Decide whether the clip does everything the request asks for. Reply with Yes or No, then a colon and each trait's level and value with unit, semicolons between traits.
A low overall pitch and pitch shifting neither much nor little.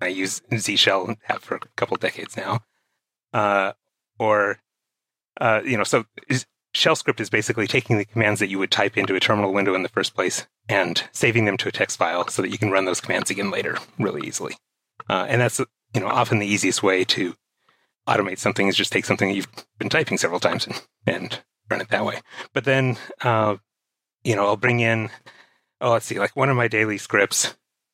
Yes: low, 105 Hz; average, 3.1 semitones